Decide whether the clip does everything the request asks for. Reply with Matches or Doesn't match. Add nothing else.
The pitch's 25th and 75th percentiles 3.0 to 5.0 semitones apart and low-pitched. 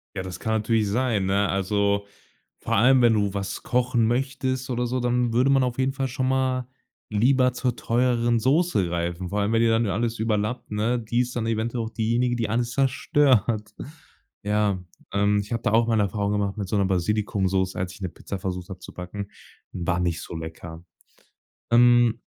Matches